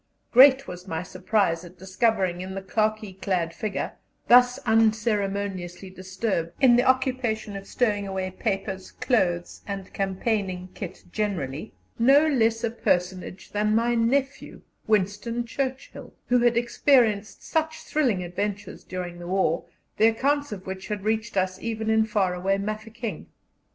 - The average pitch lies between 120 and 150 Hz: No, high, 210 Hz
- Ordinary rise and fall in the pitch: Yes, average, 3.7 semitones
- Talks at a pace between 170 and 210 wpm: No, average, 140 wpm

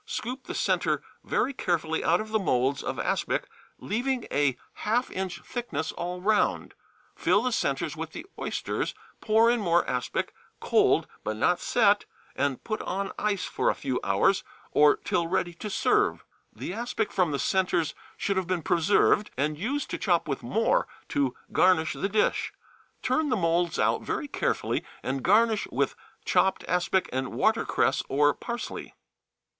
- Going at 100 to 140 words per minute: No, average, 160 wpm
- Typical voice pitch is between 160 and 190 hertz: Yes, medium, 185 Hz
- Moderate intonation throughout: No, wide, 5.7 semitones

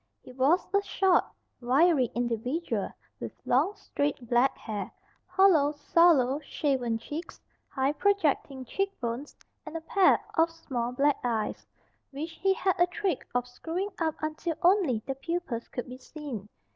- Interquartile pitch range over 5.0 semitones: Yes, wide, 5.5 semitones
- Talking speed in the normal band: Yes, average, 145 wpm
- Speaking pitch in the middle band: No, very high, 290 Hz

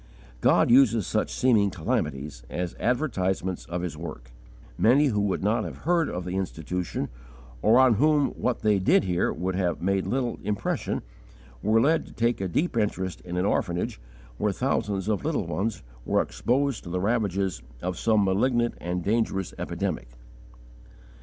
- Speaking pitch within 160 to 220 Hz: No, low, 100 Hz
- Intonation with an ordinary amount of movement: Yes, average, 4.7 semitones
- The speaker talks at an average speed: Yes, average, 160 wpm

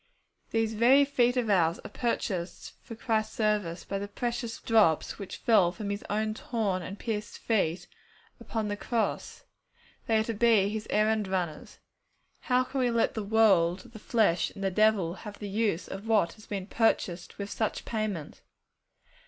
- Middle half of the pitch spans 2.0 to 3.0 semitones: Yes, average, 2.7 semitones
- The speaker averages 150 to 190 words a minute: Yes, average, 170 wpm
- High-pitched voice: Yes, high, 215 Hz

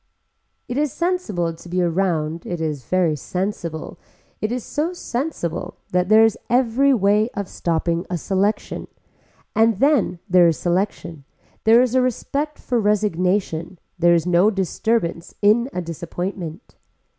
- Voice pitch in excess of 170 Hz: Yes, high, 190 Hz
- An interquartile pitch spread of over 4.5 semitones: Yes, average, 5.1 semitones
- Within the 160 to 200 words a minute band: No, average, 145 wpm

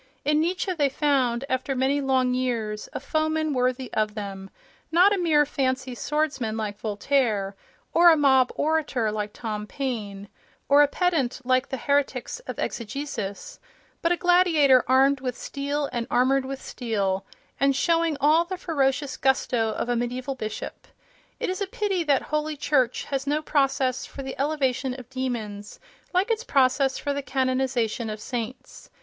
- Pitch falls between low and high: No, very high, 265 Hz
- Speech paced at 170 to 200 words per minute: No, average, 160 wpm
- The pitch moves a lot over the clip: No, average, 3.4 semitones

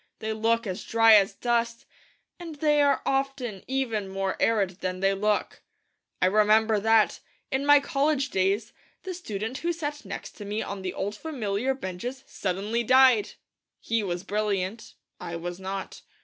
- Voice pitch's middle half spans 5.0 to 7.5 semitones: Yes, average, 5.3 semitones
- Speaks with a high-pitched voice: Yes, high, 220 Hz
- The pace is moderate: Yes, average, 160 wpm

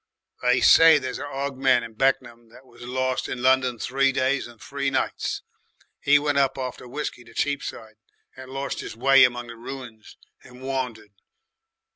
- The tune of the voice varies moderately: No, narrow, 2.1 semitones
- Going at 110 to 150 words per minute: No, average, 170 wpm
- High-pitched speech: No, low, 130 Hz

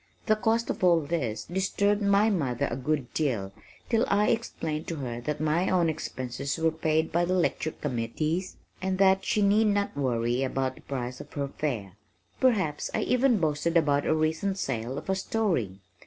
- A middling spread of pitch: No, wide, 6.3 semitones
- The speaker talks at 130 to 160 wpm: No, average, 185 wpm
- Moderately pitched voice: Yes, medium, 160 Hz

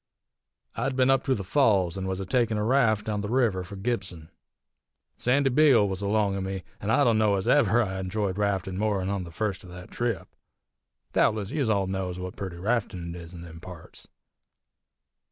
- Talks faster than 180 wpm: Yes, average, 200 wpm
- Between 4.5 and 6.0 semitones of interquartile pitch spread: No, average, 3.6 semitones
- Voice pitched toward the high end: No, low, 100 Hz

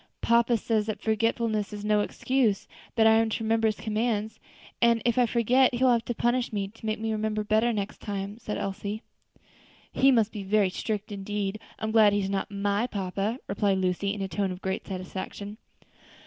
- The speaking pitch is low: No, high, 215 Hz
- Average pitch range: No, narrow, 2.1 semitones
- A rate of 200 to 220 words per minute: Yes, fast, 205 wpm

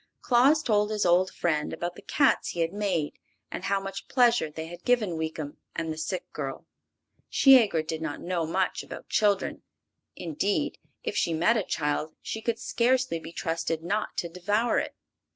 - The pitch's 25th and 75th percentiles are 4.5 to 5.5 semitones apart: Yes, average, 5.1 semitones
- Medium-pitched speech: Yes, medium, 180 Hz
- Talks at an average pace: Yes, average, 175 wpm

